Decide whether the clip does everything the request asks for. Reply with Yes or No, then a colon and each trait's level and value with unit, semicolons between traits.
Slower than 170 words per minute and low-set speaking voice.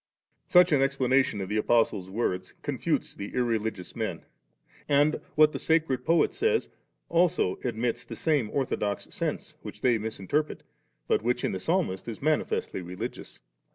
Yes: average, 155 wpm; low, 125 Hz